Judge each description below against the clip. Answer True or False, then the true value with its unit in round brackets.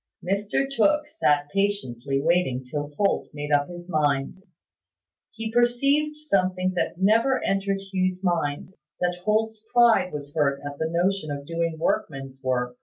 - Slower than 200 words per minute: True (150 wpm)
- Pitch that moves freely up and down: True (6.4 semitones)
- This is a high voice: False (180 Hz)